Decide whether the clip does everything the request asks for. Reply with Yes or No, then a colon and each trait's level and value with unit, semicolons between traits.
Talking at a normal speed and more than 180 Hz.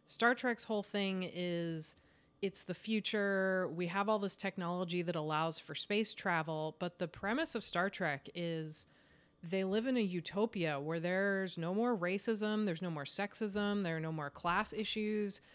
Yes: average, 175 wpm; high, 190 Hz